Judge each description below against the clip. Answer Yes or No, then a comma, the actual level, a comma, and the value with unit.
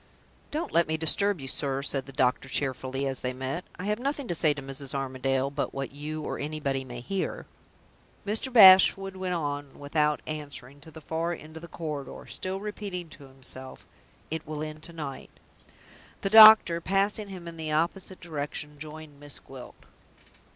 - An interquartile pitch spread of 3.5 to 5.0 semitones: Yes, average, 4.6 semitones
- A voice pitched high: No, medium, 155 Hz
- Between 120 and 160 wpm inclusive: No, average, 180 wpm